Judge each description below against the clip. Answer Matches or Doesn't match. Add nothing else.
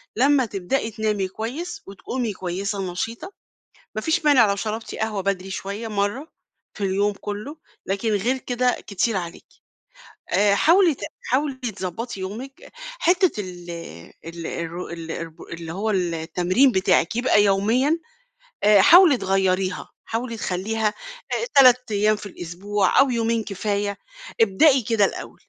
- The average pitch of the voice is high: Matches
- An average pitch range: Matches